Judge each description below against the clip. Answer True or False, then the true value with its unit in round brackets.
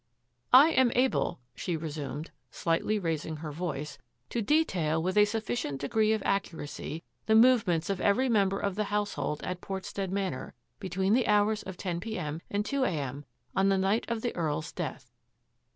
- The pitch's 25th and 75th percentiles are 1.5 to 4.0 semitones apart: False (5.1 semitones)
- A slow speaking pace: False (185 wpm)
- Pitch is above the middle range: True (195 Hz)